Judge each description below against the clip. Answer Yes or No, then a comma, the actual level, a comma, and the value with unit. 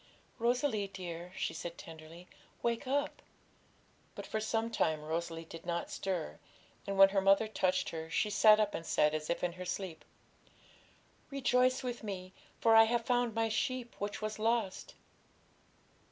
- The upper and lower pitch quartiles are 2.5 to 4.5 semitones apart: No, average, 4.9 semitones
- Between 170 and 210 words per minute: No, average, 160 wpm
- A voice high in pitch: Yes, high, 200 Hz